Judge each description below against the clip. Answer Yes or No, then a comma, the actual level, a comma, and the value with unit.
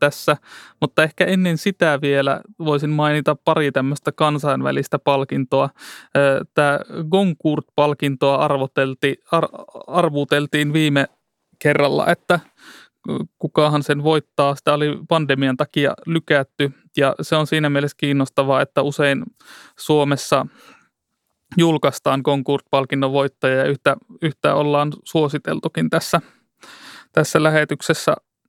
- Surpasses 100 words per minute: No, slow, 95 wpm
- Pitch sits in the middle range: Yes, medium, 145 Hz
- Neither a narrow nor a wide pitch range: No, narrow, 2.0 semitones